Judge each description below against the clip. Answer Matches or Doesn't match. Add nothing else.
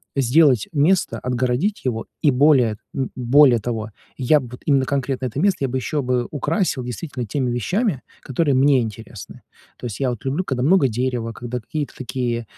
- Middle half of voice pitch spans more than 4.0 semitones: Doesn't match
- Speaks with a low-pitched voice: Matches